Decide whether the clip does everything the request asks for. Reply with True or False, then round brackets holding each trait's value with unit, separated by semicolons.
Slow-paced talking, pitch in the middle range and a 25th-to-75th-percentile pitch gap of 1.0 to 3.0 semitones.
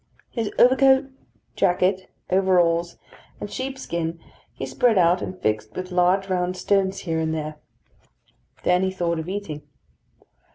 True (130 wpm; 180 Hz; 2.6 semitones)